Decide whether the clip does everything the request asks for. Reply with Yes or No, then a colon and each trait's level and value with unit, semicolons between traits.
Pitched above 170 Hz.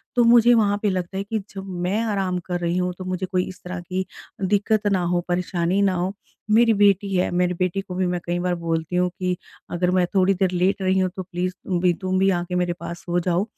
Yes: medium, 185 Hz